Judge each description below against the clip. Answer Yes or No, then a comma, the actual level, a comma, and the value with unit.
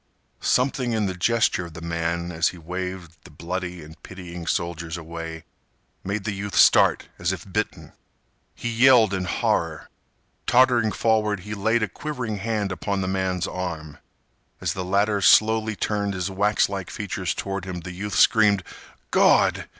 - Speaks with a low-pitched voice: Yes, very low, 95 Hz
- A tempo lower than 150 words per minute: No, average, 160 wpm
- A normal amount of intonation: Yes, average, 3.3 semitones